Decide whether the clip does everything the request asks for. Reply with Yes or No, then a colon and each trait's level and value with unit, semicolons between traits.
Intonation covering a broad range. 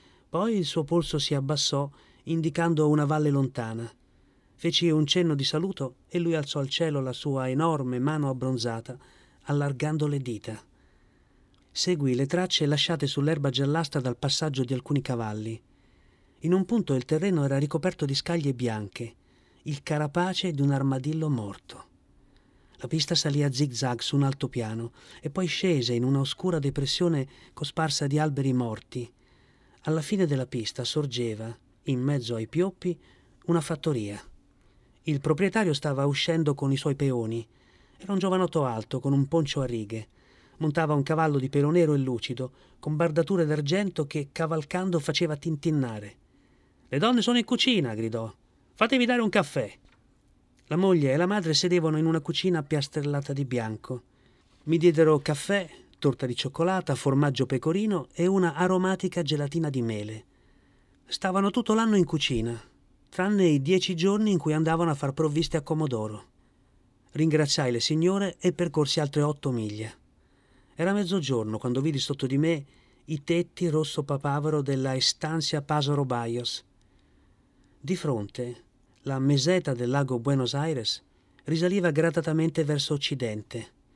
No: average, 4.5 semitones